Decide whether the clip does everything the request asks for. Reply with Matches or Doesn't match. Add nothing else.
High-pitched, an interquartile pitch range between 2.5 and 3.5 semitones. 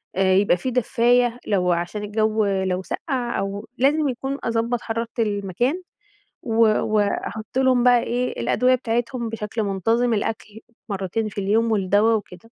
Matches